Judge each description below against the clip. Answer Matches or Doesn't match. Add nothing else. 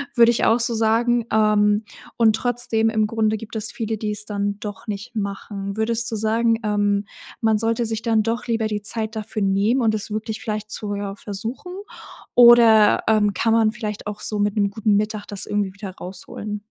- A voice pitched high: Matches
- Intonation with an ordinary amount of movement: Doesn't match